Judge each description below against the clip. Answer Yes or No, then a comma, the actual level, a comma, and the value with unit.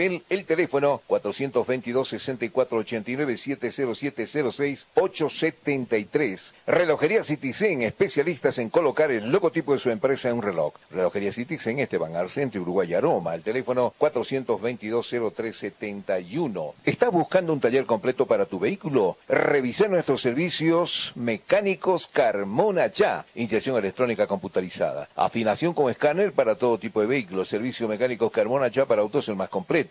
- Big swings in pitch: No, average, 4.6 semitones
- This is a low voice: Yes, low, 130 Hz